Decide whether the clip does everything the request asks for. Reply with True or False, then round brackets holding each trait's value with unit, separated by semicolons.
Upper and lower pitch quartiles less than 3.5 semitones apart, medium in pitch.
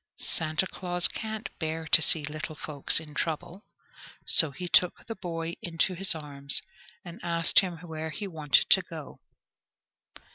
True (2.4 semitones; 165 Hz)